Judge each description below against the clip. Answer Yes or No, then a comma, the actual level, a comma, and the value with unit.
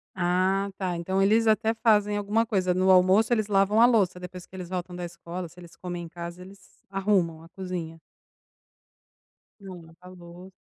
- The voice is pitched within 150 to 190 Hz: Yes, medium, 185 Hz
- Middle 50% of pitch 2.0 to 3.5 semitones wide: Yes, narrow, 2.5 semitones